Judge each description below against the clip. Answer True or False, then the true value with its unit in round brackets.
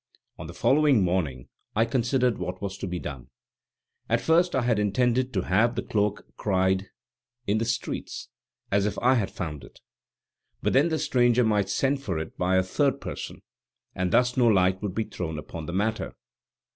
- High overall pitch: False (105 Hz)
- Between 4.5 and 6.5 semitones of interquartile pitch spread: True (5.0 semitones)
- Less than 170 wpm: False (185 wpm)